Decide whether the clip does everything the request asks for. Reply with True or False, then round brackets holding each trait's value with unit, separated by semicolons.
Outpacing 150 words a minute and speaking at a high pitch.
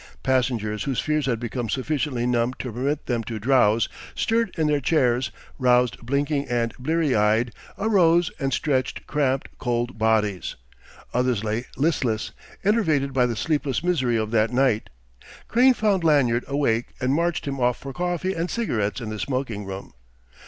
False (160 wpm; 130 Hz)